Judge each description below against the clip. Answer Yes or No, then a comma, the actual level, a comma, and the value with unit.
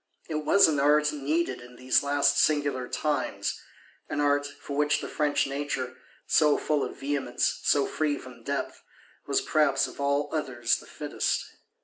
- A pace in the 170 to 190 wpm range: No, average, 160 wpm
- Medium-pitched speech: Yes, medium, 145 Hz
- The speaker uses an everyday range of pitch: No, narrow, 1.7 semitones